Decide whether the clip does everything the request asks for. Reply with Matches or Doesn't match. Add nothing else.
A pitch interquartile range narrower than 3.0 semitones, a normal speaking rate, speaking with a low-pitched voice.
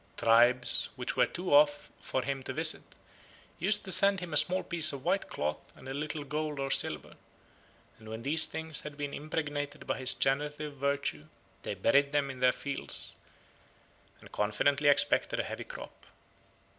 Doesn't match